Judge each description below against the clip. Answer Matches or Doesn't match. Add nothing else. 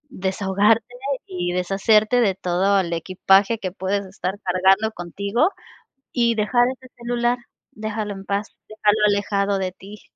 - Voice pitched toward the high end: Matches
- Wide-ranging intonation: Doesn't match